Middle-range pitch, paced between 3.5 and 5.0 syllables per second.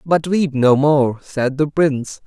Yes: medium, 145 Hz; 3.9 syllables/s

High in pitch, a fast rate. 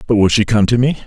No: low, 115 Hz; fast, 340 wpm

